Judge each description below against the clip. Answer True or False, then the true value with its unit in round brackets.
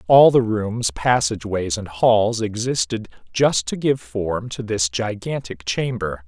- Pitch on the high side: False (110 Hz)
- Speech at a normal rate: True (145 wpm)